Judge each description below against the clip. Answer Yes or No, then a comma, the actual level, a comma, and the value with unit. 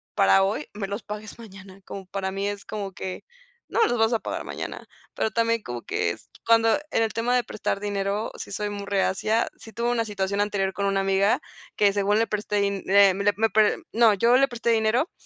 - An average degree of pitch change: No, narrow, 2.3 semitones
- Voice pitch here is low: No, high, 205 Hz